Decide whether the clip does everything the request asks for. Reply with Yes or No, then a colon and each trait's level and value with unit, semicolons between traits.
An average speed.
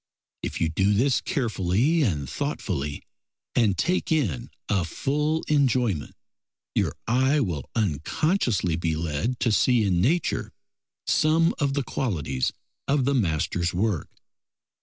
No: slow, 125 wpm